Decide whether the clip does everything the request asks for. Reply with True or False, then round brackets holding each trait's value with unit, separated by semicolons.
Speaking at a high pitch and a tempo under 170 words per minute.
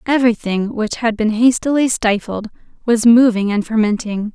True (225 Hz; 140 wpm)